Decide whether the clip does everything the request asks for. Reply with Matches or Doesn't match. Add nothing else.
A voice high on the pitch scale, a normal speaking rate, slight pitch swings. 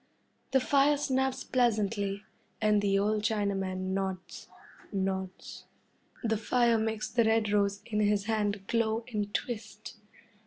Doesn't match